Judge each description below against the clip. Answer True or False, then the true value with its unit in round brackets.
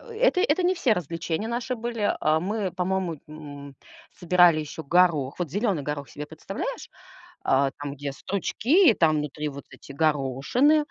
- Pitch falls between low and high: True (170 Hz)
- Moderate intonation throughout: False (6.9 semitones)